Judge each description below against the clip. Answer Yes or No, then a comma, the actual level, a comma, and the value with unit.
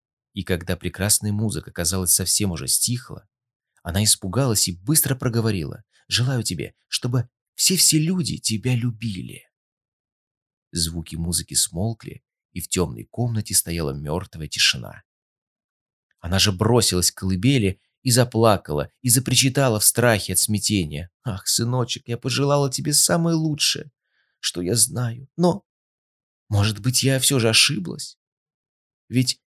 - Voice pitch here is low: Yes, low, 115 Hz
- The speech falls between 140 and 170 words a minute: No, average, 125 wpm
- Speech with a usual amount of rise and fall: No, wide, 5.9 semitones